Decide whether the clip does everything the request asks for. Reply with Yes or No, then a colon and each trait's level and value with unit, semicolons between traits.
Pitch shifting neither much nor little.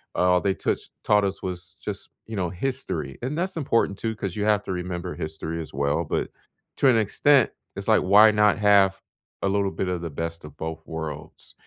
Yes: average, 4.2 semitones